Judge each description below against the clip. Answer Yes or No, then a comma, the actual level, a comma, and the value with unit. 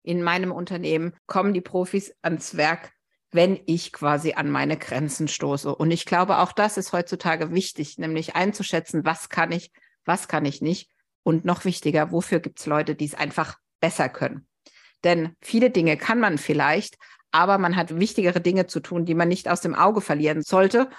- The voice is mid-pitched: Yes, medium, 170 Hz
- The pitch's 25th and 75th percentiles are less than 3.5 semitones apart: Yes, average, 2.7 semitones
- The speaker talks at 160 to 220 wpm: Yes, average, 185 wpm